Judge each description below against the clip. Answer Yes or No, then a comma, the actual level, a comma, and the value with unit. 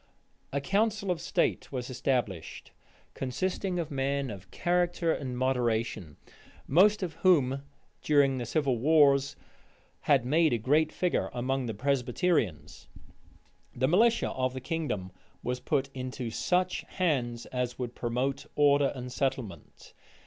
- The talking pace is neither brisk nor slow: No, slow, 130 wpm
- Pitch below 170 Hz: Yes, low, 135 Hz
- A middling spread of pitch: Yes, average, 4.6 semitones